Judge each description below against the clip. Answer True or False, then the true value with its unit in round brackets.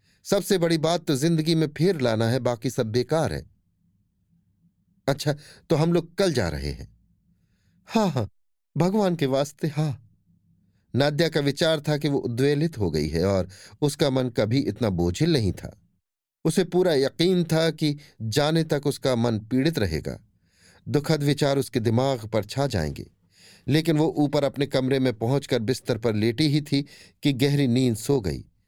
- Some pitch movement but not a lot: False (6.1 semitones)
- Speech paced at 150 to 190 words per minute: True (170 wpm)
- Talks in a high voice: False (135 Hz)